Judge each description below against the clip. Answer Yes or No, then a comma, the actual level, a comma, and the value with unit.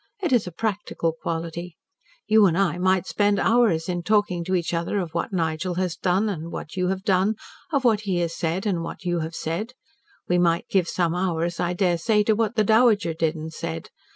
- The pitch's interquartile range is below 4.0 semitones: Yes, average, 3.5 semitones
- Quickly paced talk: Yes, fast, 215 wpm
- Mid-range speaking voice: Yes, medium, 180 Hz